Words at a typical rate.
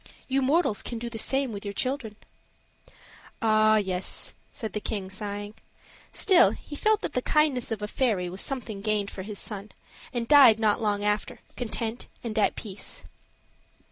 Yes: average, 170 wpm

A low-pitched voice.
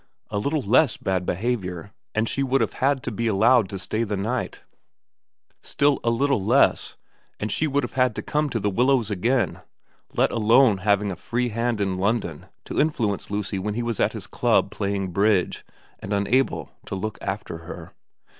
Yes: low, 110 Hz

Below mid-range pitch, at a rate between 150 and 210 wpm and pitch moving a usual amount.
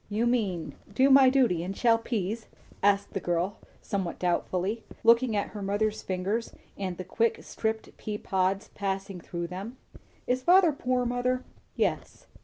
No: high, 210 Hz; average, 155 wpm; average, 4.1 semitones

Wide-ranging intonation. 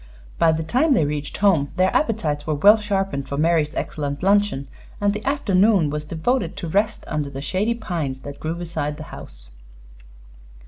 Yes: wide, 5.7 semitones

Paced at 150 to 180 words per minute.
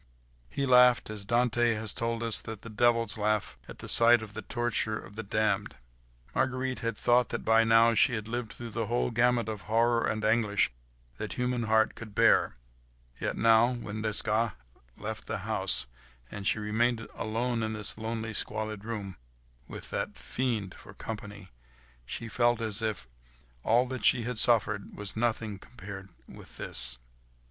Yes: average, 165 wpm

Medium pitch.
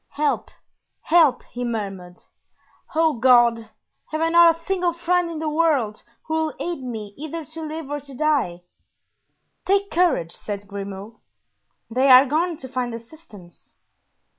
No: very high, 285 Hz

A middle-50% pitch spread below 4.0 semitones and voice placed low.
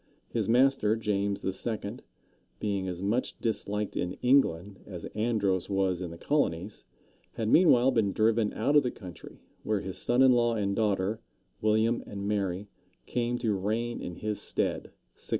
Yes: average, 3.3 semitones; low, 105 Hz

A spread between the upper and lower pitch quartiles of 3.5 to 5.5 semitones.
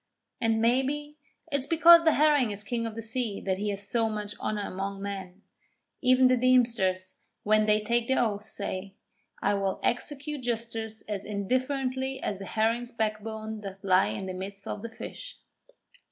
Yes: average, 4.1 semitones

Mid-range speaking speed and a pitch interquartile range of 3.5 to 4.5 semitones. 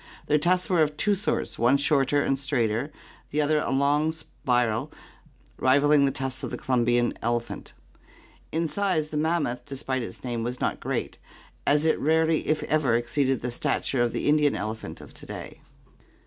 Yes: average, 175 wpm; average, 3.9 semitones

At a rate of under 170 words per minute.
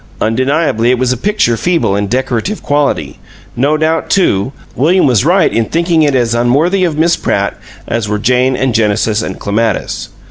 No: average, 175 wpm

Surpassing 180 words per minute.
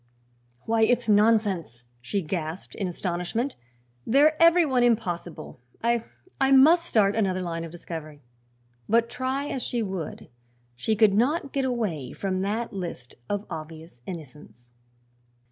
No: slow, 135 wpm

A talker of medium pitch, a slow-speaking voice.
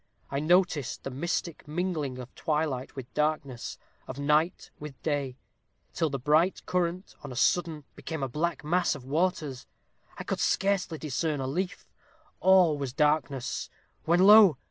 No: medium, 150 Hz; average, 150 wpm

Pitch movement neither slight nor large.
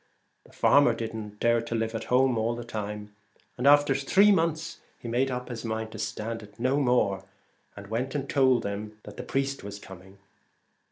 Yes: average, 3.8 semitones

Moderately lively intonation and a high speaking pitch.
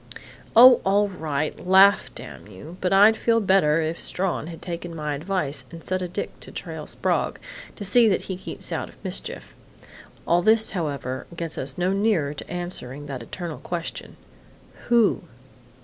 No: average, 4.4 semitones; medium, 175 Hz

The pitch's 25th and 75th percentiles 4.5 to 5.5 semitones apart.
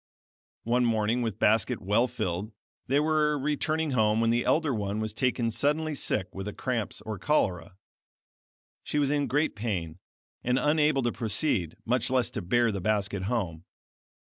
Yes: average, 5.2 semitones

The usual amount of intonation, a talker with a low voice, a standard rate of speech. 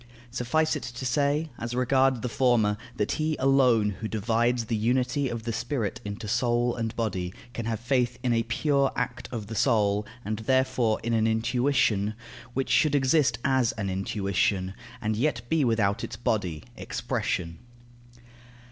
Yes: average, 3.3 semitones; low, 120 Hz; average, 160 wpm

